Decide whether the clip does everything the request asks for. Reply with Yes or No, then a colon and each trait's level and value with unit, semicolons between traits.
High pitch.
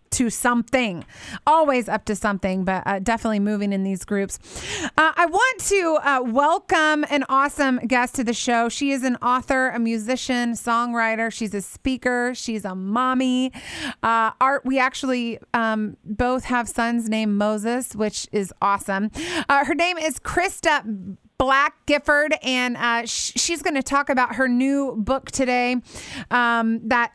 Yes: high, 245 Hz